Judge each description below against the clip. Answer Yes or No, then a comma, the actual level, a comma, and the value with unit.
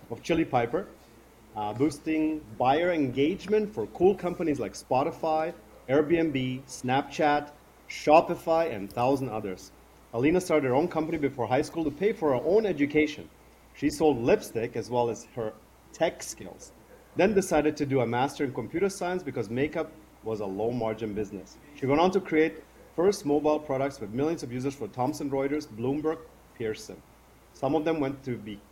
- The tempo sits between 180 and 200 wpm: No, average, 170 wpm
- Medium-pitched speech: Yes, medium, 145 Hz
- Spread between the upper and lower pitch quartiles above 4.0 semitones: Yes, average, 5.1 semitones